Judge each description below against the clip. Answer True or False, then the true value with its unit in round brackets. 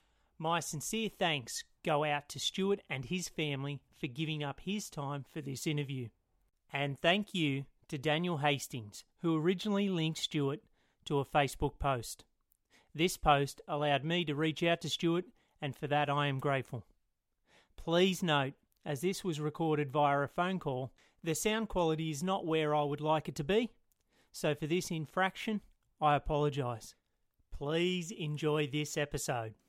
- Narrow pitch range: False (3.4 semitones)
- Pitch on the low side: False (150 Hz)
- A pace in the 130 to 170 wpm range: True (160 wpm)